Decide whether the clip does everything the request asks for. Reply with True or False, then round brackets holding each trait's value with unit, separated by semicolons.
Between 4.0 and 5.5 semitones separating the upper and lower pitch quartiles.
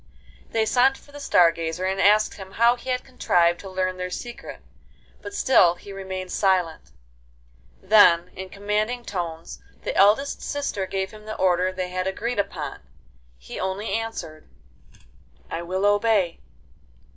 False (3.2 semitones)